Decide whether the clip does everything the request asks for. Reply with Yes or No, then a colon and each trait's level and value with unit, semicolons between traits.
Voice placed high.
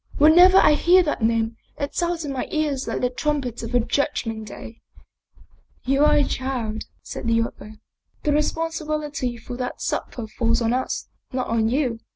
Yes: very high, 260 Hz